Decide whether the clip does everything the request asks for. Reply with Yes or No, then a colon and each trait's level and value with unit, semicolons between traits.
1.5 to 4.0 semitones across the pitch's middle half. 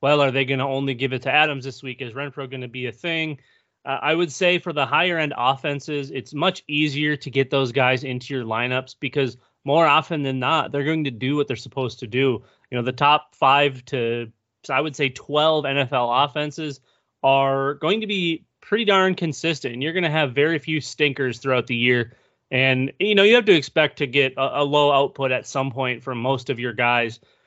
Yes: narrow, 2.6 semitones